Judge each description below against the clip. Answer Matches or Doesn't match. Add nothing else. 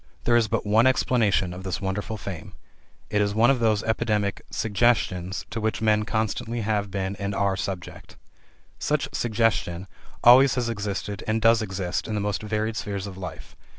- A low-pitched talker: Matches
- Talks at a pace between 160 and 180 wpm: Matches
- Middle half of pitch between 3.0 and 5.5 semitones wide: Doesn't match